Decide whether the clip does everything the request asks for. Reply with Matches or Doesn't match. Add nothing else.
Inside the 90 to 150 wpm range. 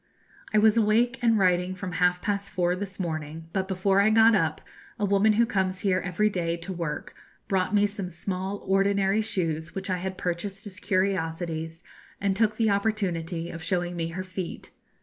Doesn't match